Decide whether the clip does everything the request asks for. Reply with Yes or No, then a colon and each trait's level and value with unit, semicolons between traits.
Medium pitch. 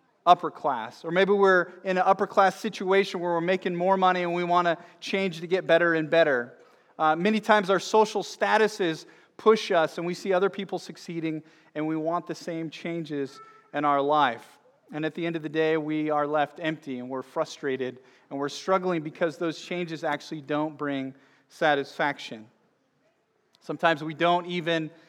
Yes: medium, 165 Hz